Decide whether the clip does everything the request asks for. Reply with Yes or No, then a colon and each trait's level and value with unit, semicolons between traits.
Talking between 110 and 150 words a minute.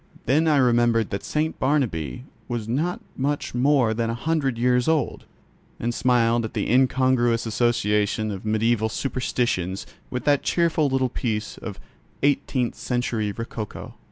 Yes: average, 140 wpm